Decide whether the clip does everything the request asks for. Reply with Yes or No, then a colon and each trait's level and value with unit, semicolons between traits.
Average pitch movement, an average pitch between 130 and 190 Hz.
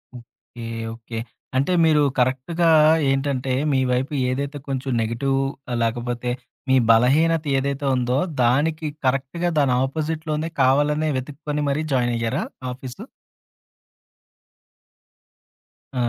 Yes: average, 3.2 semitones; low, 135 Hz